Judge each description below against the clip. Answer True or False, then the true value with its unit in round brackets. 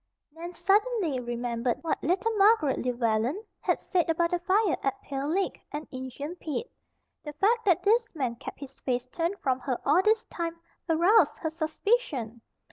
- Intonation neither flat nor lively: False (6.9 semitones)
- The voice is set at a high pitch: True (325 Hz)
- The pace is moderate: True (165 wpm)